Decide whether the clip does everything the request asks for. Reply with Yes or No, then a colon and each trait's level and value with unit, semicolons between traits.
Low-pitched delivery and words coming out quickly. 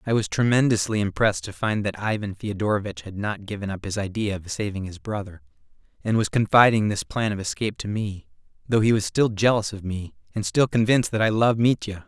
Yes: low, 105 Hz; fast, 210 wpm